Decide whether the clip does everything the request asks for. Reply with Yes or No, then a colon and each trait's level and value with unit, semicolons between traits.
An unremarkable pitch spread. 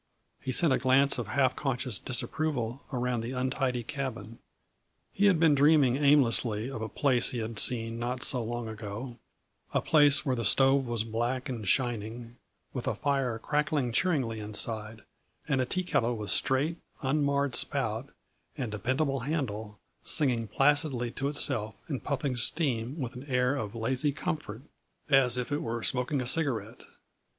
Yes: average, 3.5 semitones